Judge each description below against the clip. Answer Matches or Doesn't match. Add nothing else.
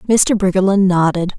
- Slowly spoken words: Matches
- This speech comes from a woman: Matches